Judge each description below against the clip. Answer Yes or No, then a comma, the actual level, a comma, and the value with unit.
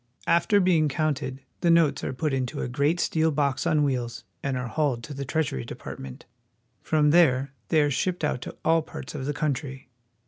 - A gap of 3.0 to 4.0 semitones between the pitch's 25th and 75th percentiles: Yes, average, 3.3 semitones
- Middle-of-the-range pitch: Yes, medium, 145 Hz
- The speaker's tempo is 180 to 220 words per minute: Yes, average, 185 wpm